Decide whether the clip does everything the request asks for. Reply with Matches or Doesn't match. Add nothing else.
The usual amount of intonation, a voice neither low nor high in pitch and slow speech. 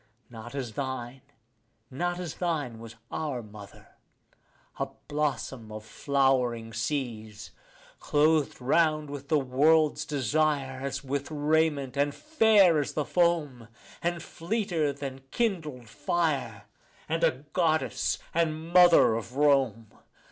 Matches